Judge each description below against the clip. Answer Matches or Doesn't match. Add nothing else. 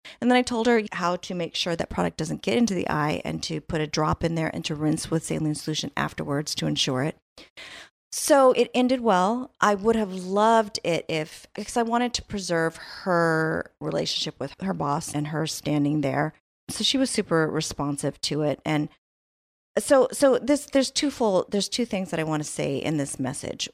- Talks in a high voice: Doesn't match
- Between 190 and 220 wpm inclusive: Matches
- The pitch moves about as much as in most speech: Doesn't match